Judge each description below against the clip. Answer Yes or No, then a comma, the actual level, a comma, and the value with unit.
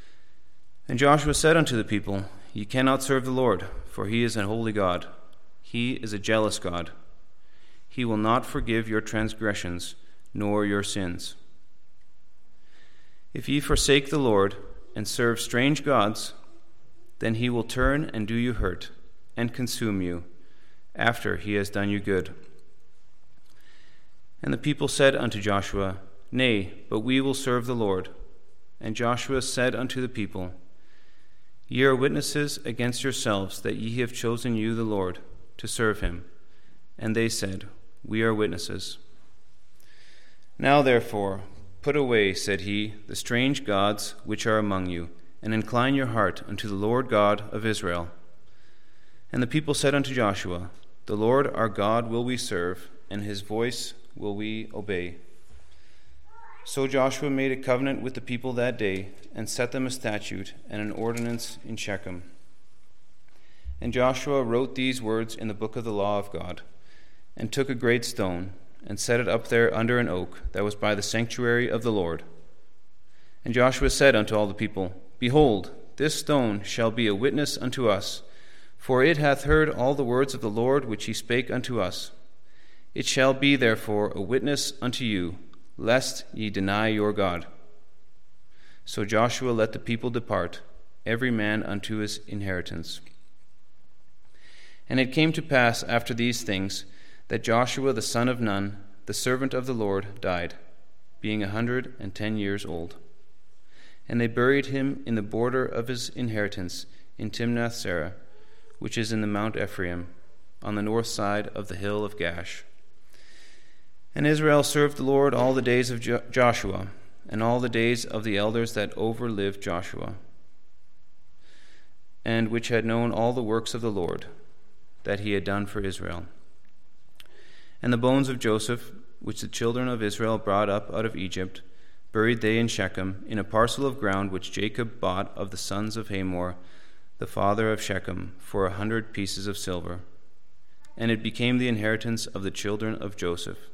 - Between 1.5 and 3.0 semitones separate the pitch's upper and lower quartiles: No, average, 3.8 semitones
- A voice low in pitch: Yes, low, 110 Hz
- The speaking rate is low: No, average, 165 wpm